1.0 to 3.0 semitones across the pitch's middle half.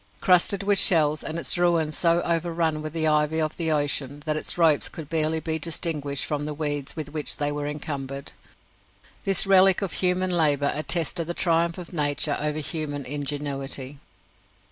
Yes: narrow, 2.5 semitones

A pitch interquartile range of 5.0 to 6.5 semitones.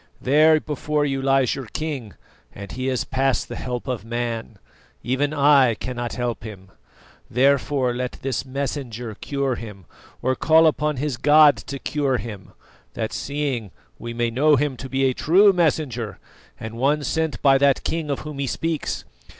No: average, 3.5 semitones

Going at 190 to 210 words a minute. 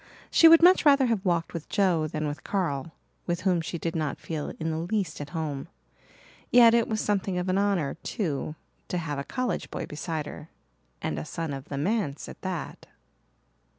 Yes: average, 195 wpm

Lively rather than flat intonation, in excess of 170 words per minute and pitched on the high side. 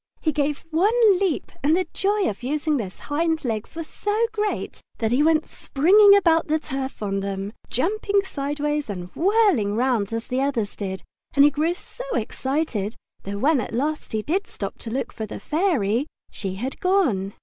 Yes: wide, 7.4 semitones; average, 185 wpm; very high, 290 Hz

